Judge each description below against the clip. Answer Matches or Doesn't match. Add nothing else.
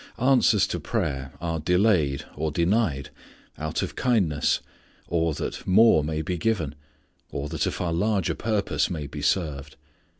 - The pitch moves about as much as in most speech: Matches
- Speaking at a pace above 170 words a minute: Doesn't match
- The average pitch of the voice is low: Matches